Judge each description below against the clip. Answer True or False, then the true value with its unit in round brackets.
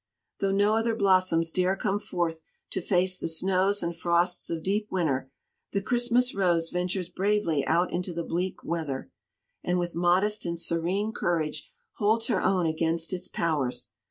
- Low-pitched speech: False (180 Hz)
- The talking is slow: False (160 wpm)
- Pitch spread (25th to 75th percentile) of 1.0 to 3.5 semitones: True (3.0 semitones)